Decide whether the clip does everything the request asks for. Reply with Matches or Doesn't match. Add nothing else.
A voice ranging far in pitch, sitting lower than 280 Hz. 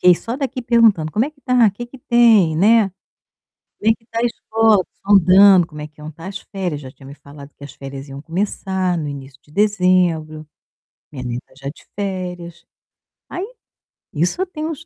Matches